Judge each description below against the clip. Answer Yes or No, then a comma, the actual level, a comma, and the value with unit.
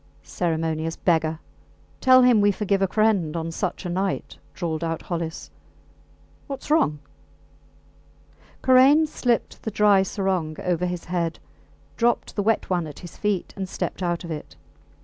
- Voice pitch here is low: No, medium, 180 Hz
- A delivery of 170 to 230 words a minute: No, average, 150 wpm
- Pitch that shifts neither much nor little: Yes, average, 4.2 semitones